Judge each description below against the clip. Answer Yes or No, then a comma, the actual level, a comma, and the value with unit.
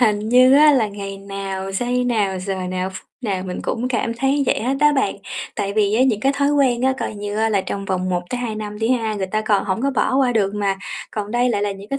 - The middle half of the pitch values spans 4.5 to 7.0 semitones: No, average, 4.0 semitones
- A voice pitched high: Yes, high, 215 Hz